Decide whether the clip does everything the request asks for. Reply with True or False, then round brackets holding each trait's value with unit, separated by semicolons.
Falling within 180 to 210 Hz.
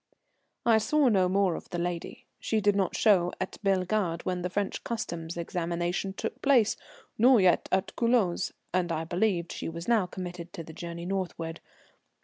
True (185 Hz)